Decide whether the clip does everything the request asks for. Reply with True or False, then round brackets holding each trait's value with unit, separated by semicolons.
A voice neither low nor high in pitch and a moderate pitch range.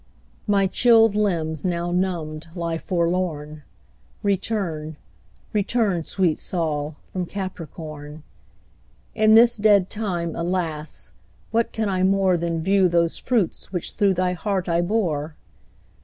True (180 Hz; 3.6 semitones)